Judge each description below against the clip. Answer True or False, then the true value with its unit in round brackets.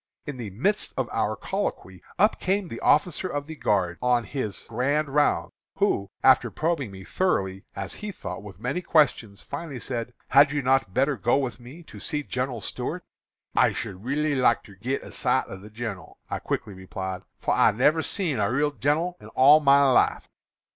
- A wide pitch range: True (6.0 semitones)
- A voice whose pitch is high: False (130 Hz)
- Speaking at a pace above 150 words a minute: True (190 wpm)